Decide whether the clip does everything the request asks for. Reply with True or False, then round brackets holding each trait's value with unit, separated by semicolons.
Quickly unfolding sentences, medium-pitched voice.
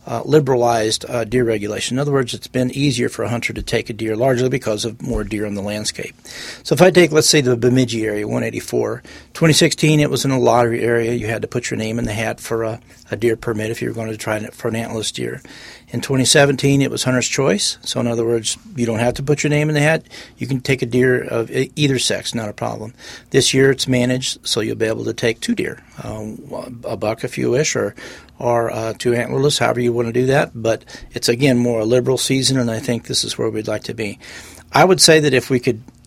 False (255 wpm; 120 Hz)